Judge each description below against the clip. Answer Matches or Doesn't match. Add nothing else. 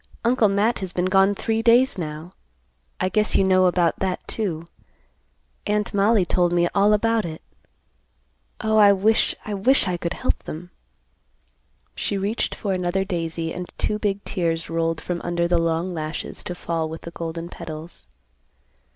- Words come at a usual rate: Matches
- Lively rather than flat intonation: Doesn't match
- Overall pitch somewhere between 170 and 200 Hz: Matches